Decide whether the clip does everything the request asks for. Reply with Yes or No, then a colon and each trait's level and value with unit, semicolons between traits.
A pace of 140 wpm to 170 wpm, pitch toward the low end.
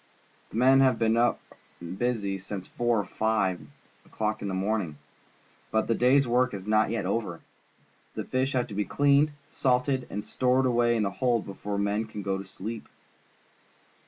No: average, 185 wpm; low, 110 Hz